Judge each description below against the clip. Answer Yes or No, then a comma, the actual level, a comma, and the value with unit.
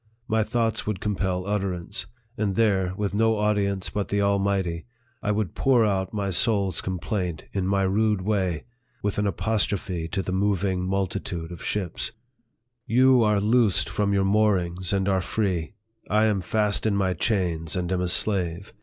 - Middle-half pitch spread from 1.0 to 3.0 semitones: Yes, narrow, 2.5 semitones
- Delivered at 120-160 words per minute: No, average, 170 wpm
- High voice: No, low, 100 Hz